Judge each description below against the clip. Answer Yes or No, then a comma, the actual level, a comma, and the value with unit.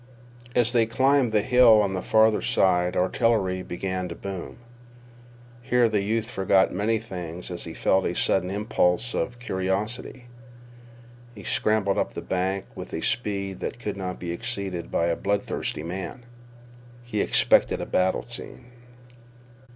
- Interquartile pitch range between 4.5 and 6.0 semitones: No, average, 3.6 semitones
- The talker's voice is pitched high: No, low, 100 Hz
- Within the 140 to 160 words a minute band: Yes, average, 150 wpm